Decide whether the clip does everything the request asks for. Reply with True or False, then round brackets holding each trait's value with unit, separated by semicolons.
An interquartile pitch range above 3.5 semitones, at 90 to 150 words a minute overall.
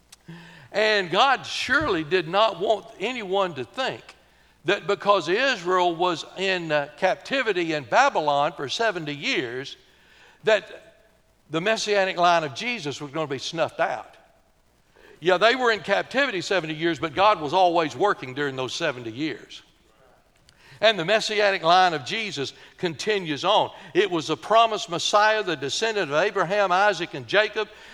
True (5.2 semitones; 145 wpm)